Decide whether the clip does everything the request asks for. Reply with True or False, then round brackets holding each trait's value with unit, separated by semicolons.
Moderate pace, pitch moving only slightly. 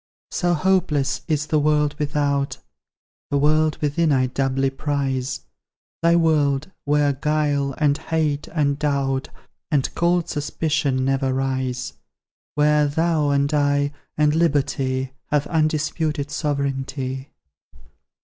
False (110 wpm; 2.0 semitones)